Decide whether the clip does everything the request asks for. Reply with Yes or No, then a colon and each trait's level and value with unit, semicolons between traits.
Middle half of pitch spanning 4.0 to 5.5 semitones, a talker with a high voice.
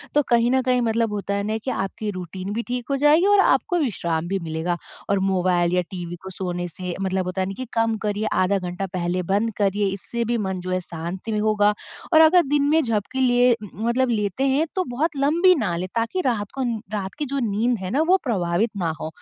Yes: average, 5.2 semitones; high, 210 Hz